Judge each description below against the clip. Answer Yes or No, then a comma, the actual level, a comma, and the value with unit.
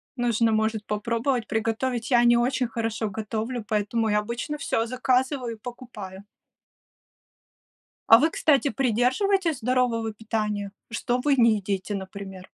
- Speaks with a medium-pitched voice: No, high, 230 Hz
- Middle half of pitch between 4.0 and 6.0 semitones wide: No, average, 2.8 semitones